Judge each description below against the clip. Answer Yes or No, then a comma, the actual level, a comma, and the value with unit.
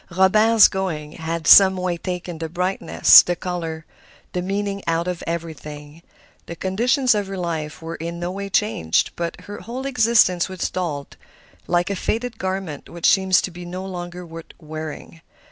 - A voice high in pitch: No, medium, 180 Hz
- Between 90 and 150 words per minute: No, average, 165 wpm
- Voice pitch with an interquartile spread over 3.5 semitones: No, average, 2.7 semitones